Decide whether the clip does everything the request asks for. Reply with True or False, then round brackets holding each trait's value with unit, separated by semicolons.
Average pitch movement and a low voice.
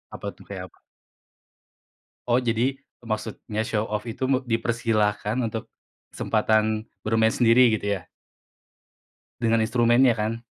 False (1.7 semitones; 115 Hz)